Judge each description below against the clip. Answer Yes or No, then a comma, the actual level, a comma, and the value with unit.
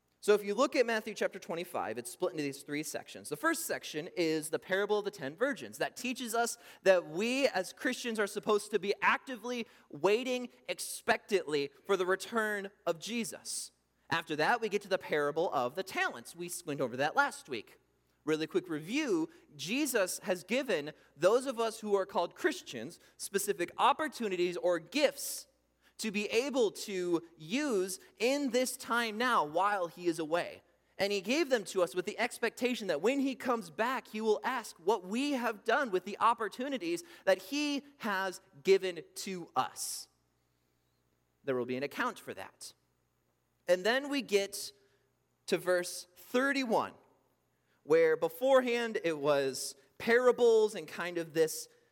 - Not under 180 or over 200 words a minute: No, average, 165 wpm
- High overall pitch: Yes, high, 205 Hz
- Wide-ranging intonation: Yes, wide, 6.3 semitones